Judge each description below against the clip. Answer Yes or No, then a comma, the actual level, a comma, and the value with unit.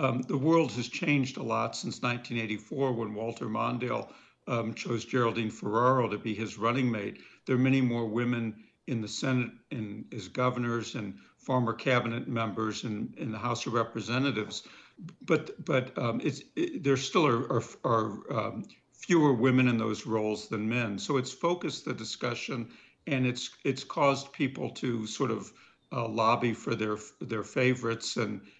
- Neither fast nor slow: Yes, average, 170 wpm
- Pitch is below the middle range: Yes, low, 120 Hz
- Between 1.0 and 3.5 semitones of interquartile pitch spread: Yes, average, 2.7 semitones